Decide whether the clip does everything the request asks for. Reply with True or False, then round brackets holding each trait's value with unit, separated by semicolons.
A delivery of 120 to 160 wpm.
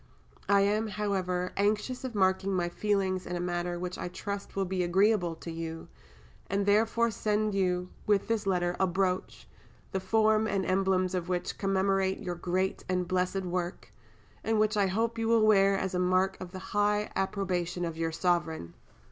False (180 wpm)